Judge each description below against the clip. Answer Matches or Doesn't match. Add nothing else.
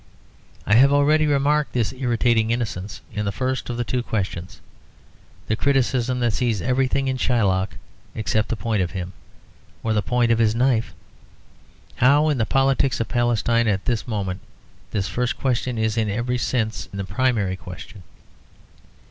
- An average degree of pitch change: Matches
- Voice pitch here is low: Matches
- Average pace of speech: Matches